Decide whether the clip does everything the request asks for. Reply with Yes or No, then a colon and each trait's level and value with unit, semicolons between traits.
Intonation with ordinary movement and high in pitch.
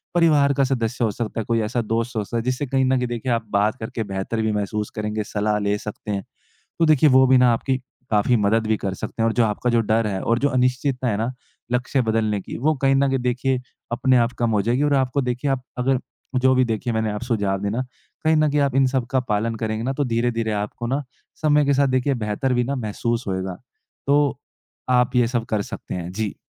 No: average, 3.4 semitones; low, 120 Hz